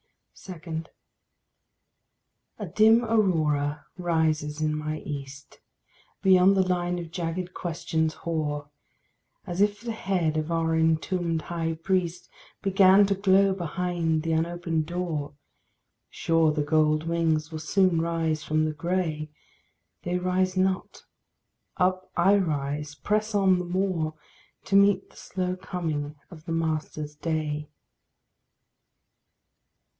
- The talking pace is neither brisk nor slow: No, slow, 120 wpm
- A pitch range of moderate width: Yes, average, 3.0 semitones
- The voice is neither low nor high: Yes, medium, 165 Hz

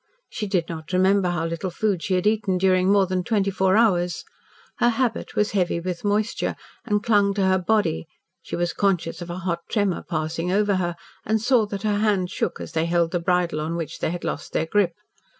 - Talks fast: Yes, fast, 215 wpm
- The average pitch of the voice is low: No, medium, 185 Hz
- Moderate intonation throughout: Yes, average, 3.1 semitones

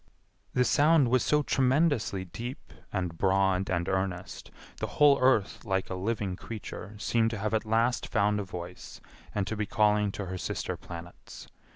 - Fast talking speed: No, average, 170 wpm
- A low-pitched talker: Yes, low, 105 Hz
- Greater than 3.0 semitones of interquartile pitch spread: Yes, average, 3.9 semitones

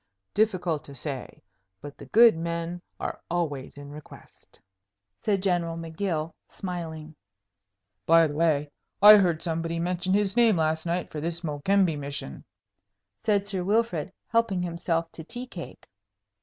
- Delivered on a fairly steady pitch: No, average, 3.4 semitones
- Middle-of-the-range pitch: Yes, medium, 170 Hz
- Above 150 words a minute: No, average, 140 wpm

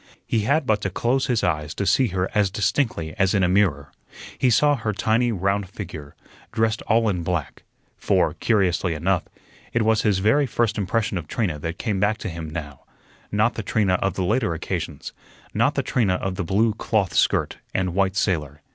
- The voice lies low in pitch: Yes, low, 100 Hz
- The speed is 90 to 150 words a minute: No, average, 195 wpm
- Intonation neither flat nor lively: Yes, average, 3.8 semitones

